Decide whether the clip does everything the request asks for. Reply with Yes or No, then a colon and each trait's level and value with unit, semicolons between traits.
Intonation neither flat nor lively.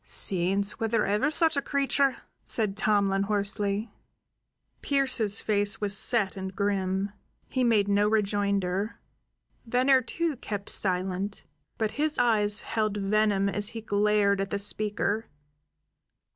No: narrow, 2.2 semitones